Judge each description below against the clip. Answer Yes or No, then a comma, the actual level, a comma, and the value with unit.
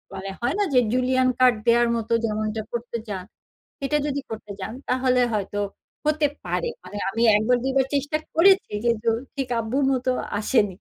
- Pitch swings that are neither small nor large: Yes, average, 3.6 semitones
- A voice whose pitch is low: No, very high, 250 Hz